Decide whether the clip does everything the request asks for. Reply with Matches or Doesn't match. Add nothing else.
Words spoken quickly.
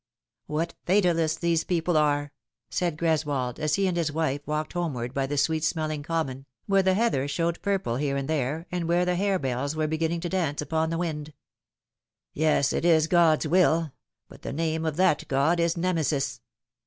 Doesn't match